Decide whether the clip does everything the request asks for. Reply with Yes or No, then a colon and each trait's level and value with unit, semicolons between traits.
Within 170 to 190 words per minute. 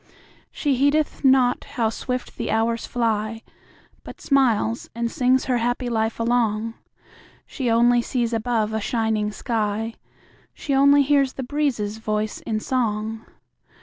No: slow, 135 wpm